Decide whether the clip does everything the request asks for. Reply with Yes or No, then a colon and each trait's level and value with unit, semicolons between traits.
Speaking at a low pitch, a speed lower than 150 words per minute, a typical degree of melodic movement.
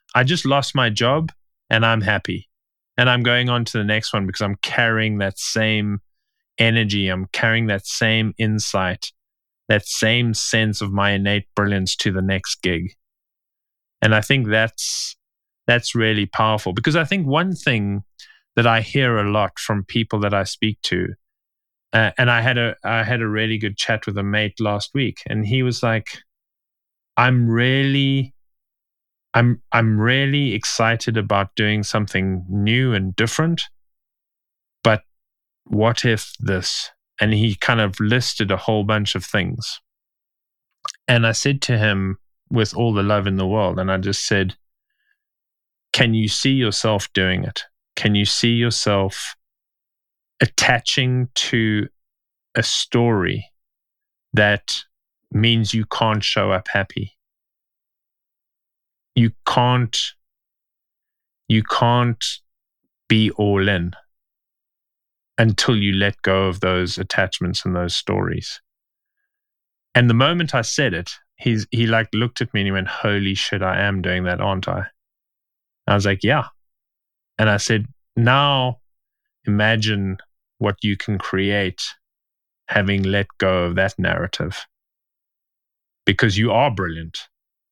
Yes: low, 110 Hz; average, 140 wpm; average, 3.1 semitones